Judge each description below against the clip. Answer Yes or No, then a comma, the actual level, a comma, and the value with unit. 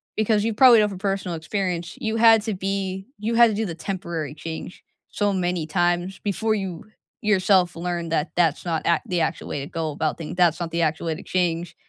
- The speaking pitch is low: No, medium, 180 Hz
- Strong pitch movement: No, average, 3.5 semitones